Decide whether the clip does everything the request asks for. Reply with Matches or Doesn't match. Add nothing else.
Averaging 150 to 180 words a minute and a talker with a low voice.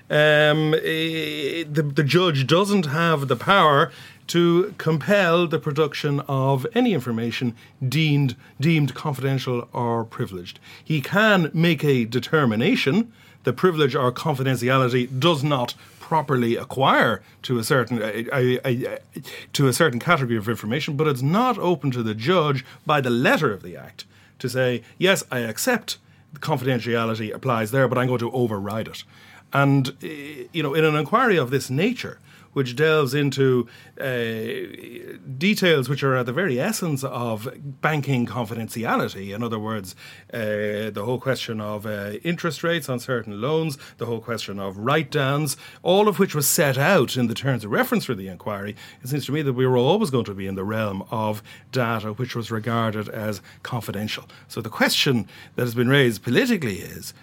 Matches